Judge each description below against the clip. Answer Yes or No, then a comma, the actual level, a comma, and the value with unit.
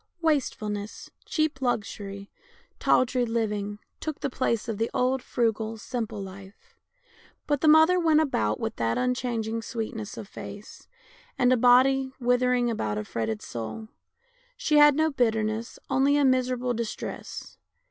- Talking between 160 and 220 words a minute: No, slow, 135 wpm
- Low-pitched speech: No, high, 240 Hz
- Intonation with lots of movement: No, average, 3.9 semitones